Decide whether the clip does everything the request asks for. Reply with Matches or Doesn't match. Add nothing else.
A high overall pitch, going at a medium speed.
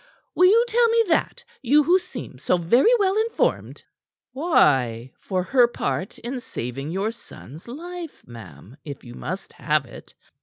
Matches